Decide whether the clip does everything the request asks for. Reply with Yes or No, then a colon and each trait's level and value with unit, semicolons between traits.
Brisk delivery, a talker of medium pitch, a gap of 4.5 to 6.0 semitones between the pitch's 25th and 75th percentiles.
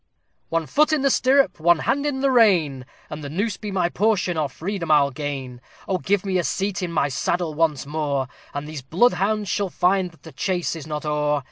Yes: fast, 215 wpm; medium, 170 Hz; average, 5.1 semitones